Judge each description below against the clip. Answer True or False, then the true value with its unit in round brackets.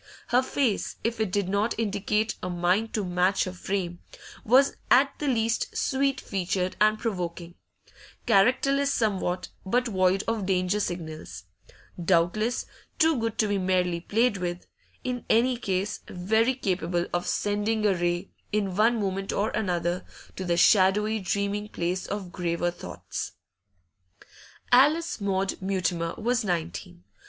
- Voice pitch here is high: True (200 Hz)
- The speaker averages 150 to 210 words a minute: False (140 wpm)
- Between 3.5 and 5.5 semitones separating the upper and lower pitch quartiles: True (3.9 semitones)